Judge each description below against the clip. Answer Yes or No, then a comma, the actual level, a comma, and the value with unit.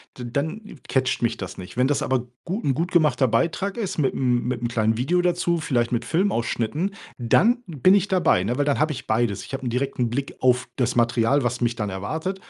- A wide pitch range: Yes, wide, 6.2 semitones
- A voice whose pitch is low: Yes, low, 130 Hz